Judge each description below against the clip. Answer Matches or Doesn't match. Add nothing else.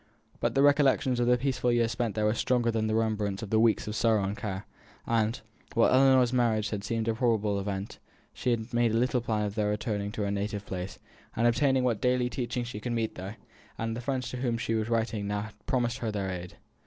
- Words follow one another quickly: Matches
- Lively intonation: Doesn't match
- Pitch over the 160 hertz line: Doesn't match